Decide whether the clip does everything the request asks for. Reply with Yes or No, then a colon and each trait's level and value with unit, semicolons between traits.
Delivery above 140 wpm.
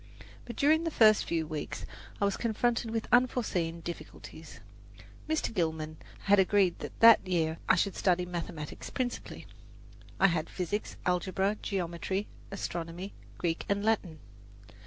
No: slow, 135 wpm